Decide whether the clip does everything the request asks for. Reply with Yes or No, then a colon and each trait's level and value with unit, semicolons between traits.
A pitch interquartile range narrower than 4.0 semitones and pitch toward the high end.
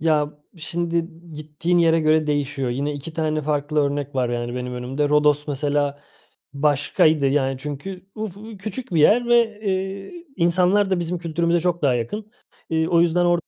No: average, 3.6 semitones; medium, 155 Hz